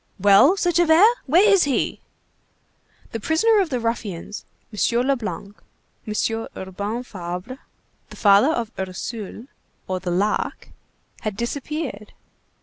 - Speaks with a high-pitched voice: Yes, high, 230 Hz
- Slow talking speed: Yes, slow, 120 wpm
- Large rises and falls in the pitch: Yes, wide, 6.5 semitones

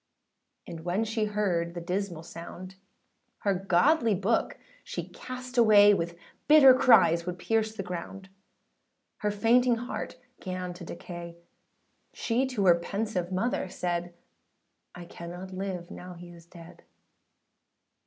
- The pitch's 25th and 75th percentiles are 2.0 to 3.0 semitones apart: No, average, 4.1 semitones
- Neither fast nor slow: No, slow, 130 wpm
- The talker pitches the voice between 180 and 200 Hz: Yes, medium, 185 Hz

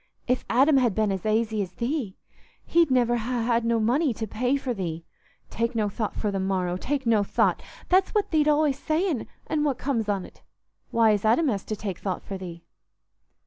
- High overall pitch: Yes, high, 230 Hz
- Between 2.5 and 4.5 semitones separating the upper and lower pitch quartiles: No, average, 5.0 semitones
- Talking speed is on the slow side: No, average, 190 wpm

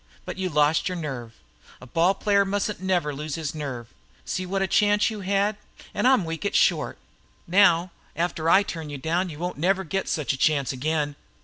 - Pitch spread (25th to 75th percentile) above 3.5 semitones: Yes, average, 4.4 semitones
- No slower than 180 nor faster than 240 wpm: Yes, average, 195 wpm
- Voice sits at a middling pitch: Yes, medium, 170 Hz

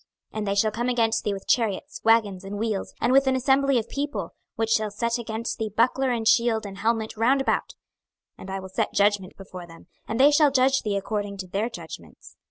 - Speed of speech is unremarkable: No, fast, 220 wpm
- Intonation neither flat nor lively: Yes, average, 3.6 semitones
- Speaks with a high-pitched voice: Yes, high, 225 Hz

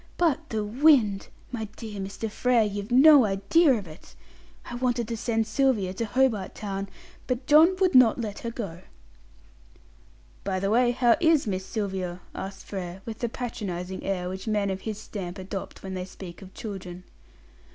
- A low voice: No, high, 210 Hz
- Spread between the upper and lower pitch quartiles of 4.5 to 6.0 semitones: No, average, 4.1 semitones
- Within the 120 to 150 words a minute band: No, average, 170 wpm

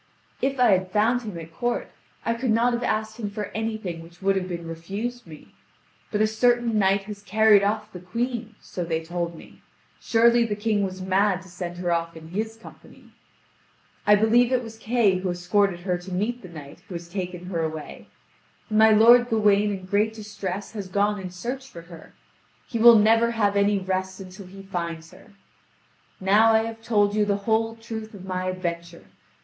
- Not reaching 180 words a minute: No, average, 200 wpm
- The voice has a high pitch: Yes, high, 205 Hz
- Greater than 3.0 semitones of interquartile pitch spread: Yes, average, 3.5 semitones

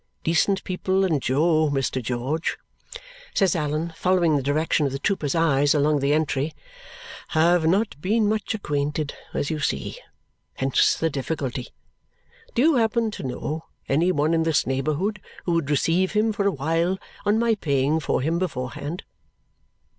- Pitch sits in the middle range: Yes, medium, 160 Hz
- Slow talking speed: No, average, 155 wpm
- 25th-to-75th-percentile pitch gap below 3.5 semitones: No, average, 4.5 semitones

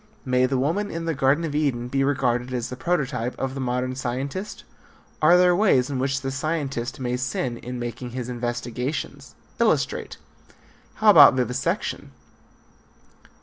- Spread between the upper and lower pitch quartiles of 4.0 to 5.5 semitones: No, average, 2.9 semitones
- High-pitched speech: No, low, 130 Hz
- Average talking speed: Yes, average, 150 wpm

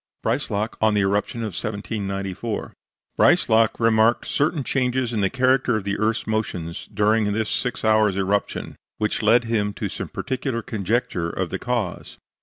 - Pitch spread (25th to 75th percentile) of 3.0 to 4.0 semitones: No, narrow, 2.5 semitones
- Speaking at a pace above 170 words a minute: No, average, 155 wpm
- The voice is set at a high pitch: No, low, 110 Hz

